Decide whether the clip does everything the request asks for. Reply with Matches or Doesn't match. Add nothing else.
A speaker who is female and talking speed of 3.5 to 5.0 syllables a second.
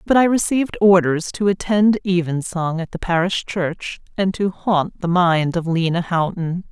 Matches